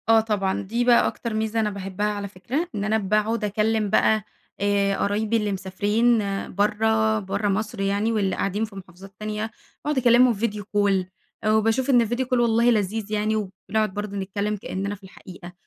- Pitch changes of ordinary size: No, narrow, 2.0 semitones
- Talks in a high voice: Yes, high, 210 Hz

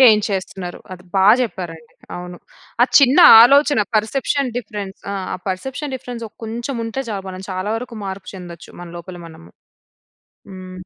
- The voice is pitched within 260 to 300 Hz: No, high, 200 Hz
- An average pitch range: Yes, average, 5.0 semitones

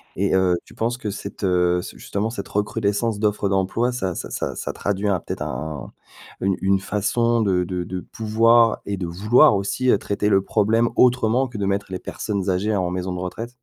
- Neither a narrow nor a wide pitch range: Yes, average, 3.2 semitones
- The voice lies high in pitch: No, low, 100 Hz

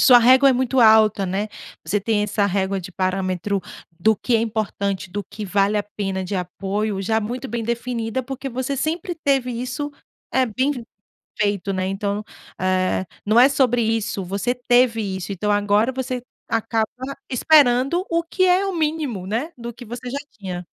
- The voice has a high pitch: Yes, high, 225 Hz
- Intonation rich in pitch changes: No, average, 4.2 semitones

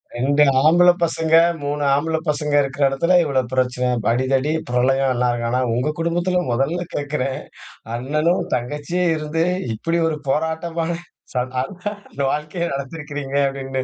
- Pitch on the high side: No, medium, 145 Hz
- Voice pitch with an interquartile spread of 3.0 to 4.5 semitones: Yes, average, 3.6 semitones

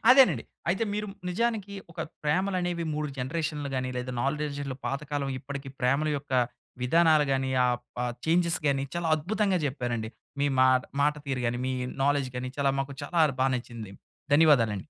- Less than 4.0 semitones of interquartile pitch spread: No, average, 4.3 semitones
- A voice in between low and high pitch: Yes, medium, 145 Hz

